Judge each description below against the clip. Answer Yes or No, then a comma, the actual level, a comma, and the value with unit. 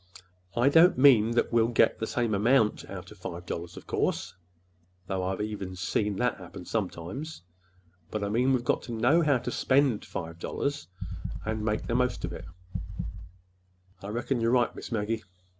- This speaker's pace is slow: No, average, 170 wpm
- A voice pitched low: Yes, low, 105 Hz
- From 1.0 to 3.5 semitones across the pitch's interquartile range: No, average, 4.9 semitones